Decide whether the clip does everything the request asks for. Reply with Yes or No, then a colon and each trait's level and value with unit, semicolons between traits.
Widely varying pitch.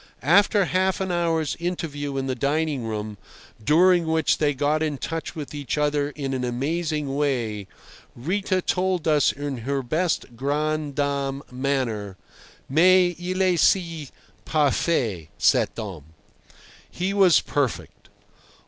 No: average, 4.1 semitones